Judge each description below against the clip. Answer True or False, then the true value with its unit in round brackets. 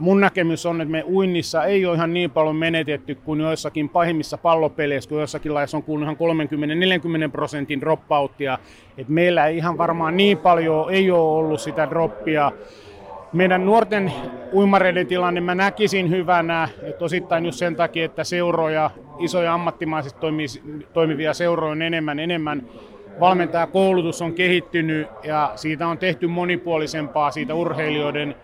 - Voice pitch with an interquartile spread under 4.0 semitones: True (2.4 semitones)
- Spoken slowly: False (140 wpm)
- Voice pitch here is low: False (165 Hz)